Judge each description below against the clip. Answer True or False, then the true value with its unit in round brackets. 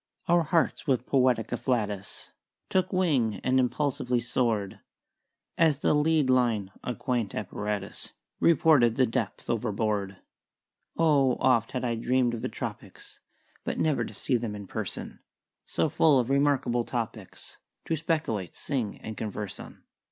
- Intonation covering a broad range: False (4.4 semitones)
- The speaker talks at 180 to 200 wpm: False (140 wpm)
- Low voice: True (125 Hz)